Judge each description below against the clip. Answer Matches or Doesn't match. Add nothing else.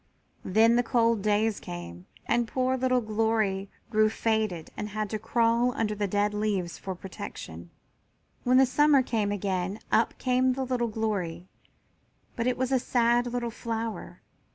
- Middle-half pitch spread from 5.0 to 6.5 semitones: Doesn't match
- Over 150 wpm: Matches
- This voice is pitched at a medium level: Doesn't match